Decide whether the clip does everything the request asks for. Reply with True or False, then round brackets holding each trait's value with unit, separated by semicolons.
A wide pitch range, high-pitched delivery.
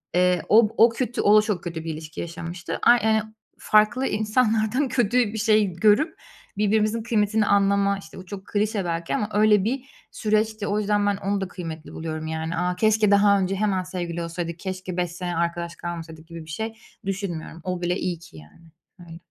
False (3.8 semitones; 195 Hz)